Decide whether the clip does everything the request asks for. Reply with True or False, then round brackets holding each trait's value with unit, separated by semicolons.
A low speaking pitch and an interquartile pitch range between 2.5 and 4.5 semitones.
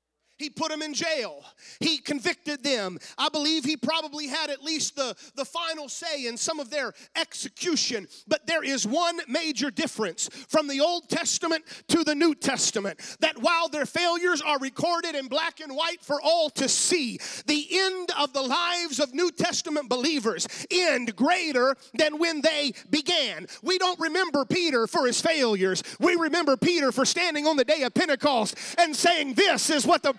False (305 Hz; 3.4 semitones)